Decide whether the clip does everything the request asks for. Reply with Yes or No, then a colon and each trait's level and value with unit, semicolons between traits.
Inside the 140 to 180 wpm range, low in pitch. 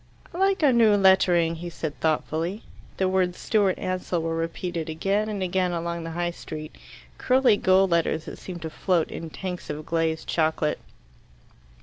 No: average, 165 wpm; medium, 175 Hz